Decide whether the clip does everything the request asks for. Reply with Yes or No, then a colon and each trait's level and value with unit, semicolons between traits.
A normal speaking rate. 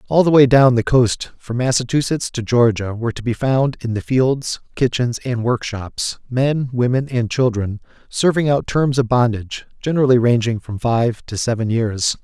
Yes: average, 175 wpm